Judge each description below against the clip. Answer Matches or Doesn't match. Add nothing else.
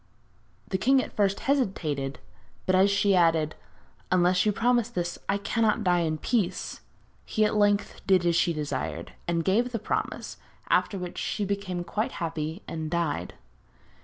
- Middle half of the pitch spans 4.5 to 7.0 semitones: Doesn't match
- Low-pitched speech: Doesn't match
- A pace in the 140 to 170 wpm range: Matches